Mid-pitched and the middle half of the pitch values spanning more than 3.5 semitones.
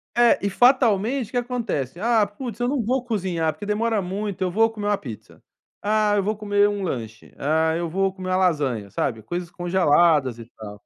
No: high, 195 Hz; average, 5.2 semitones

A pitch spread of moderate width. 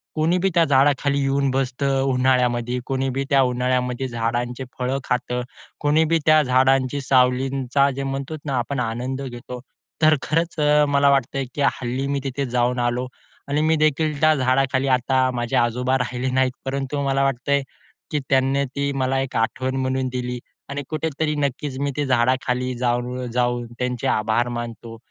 No: narrow, 2.0 semitones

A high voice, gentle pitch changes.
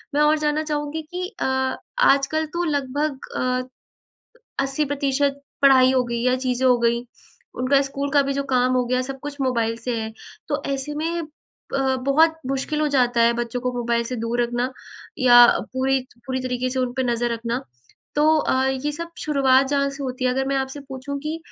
Yes: very high, 265 Hz; narrow, 2.2 semitones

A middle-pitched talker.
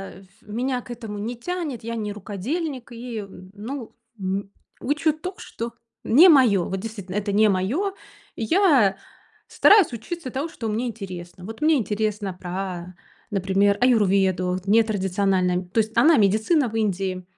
No: high, 215 Hz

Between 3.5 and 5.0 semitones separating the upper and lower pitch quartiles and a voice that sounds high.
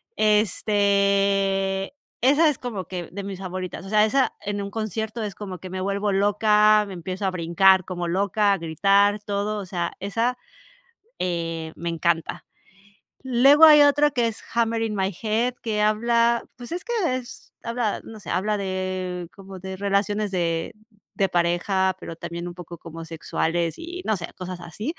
No: average, 3.0 semitones; high, 200 Hz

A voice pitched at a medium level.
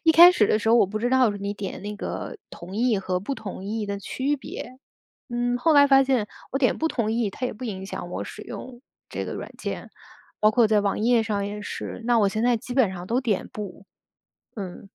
No: high, 220 Hz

